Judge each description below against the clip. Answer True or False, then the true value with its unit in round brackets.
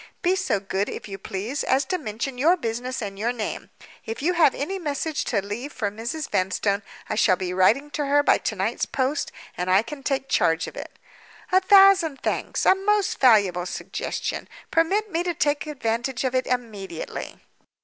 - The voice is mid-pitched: False (255 Hz)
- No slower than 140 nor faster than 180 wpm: False (190 wpm)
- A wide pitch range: True (6.9 semitones)